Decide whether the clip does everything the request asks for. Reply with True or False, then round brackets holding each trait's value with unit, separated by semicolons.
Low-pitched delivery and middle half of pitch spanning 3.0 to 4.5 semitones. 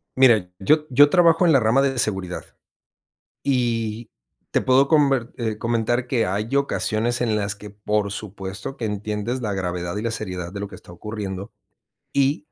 True (110 Hz; 4.2 semitones)